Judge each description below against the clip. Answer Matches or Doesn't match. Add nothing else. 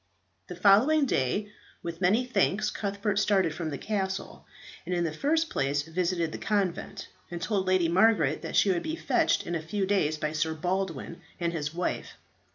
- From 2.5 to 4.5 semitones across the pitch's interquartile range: Matches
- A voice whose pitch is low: Doesn't match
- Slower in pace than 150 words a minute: Doesn't match